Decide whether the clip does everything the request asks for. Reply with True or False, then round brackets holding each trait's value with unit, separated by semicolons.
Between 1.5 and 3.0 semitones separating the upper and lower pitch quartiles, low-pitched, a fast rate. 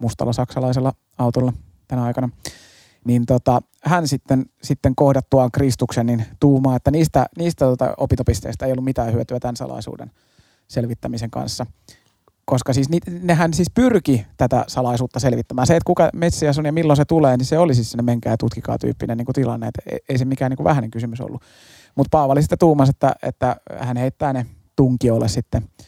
True (2.7 semitones; 130 Hz; 170 wpm)